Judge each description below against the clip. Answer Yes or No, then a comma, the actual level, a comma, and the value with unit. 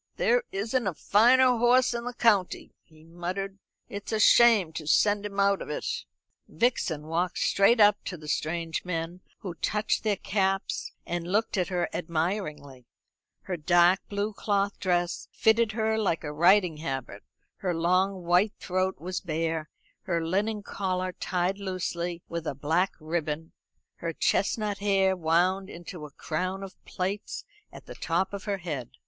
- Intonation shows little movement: No, average, 3.4 semitones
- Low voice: No, medium, 185 Hz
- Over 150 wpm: Yes, average, 160 wpm